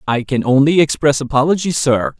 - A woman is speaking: No, male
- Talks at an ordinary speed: Yes, average, 165 wpm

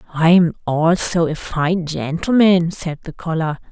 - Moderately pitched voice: Yes, medium, 165 Hz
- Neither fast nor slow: Yes, average, 145 wpm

